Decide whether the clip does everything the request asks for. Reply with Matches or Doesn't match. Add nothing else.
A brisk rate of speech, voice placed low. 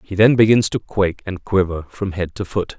Matches